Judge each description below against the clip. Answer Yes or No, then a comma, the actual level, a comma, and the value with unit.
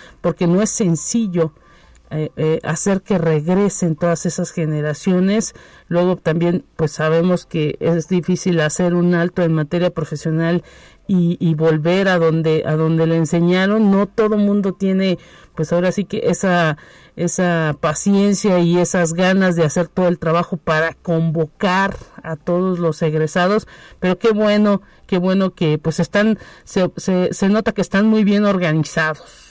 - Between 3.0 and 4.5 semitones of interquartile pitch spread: No, narrow, 2.6 semitones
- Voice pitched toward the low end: No, medium, 175 Hz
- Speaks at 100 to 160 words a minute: Yes, average, 155 wpm